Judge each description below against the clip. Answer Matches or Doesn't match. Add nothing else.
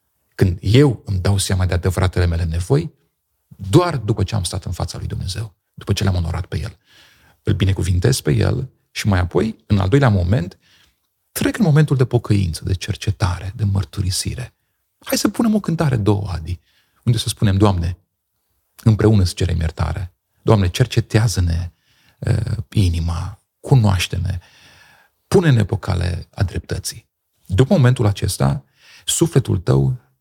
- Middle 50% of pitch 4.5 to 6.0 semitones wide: Doesn't match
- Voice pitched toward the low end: Matches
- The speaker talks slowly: Doesn't match